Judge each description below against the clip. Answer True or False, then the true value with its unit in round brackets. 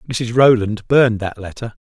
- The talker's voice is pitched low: True (115 Hz)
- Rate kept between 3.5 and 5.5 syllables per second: True (5.1 syllables/s)